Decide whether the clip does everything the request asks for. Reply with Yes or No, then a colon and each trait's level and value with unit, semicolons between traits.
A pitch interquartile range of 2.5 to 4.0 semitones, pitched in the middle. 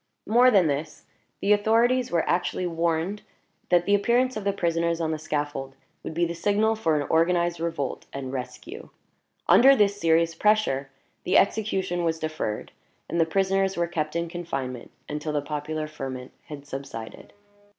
No: average, 4.9 semitones; medium, 170 Hz